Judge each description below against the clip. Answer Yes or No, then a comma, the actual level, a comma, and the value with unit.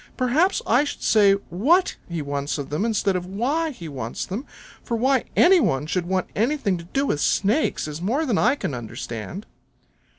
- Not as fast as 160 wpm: No, average, 190 wpm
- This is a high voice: Yes, high, 205 Hz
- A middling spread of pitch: No, wide, 8.5 semitones